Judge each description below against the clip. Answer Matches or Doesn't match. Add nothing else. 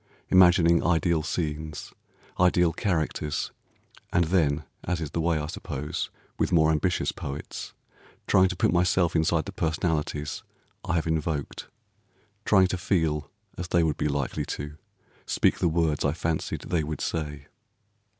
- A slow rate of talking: Doesn't match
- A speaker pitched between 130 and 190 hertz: Doesn't match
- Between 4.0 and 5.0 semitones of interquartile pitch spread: Doesn't match